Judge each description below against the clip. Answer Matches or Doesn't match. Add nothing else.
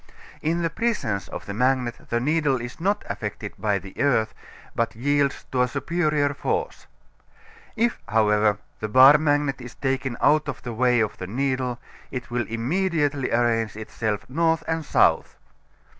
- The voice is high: Doesn't match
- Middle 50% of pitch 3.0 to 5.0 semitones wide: Matches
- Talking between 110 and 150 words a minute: Doesn't match